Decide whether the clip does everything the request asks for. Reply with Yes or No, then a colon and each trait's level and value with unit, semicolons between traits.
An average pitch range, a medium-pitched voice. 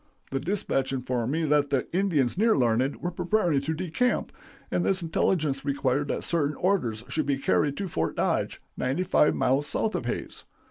Yes: average, 4.8 semitones; medium, 145 Hz